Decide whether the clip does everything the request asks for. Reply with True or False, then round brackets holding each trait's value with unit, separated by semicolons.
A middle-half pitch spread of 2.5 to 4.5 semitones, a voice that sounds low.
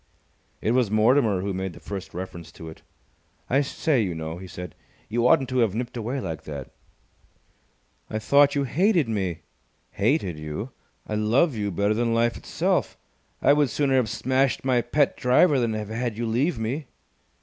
False (5.0 semitones; 115 Hz)